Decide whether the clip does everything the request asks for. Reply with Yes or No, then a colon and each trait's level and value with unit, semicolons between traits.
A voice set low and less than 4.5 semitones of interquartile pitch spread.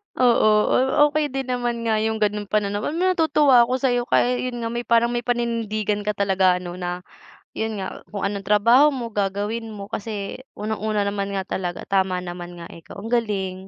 No: high, 215 Hz; average, 3.3 semitones